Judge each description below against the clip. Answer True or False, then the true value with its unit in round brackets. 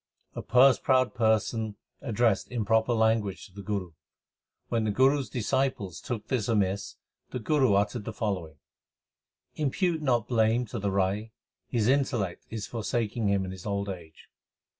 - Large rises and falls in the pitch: False (3.6 semitones)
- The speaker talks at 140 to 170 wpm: True (160 wpm)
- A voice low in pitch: True (110 Hz)